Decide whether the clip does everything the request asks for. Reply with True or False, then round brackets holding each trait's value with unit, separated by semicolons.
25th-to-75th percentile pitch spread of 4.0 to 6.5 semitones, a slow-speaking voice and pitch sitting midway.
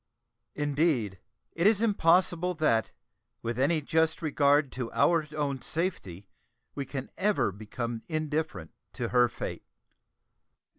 True (5.2 semitones; 115 wpm; 145 Hz)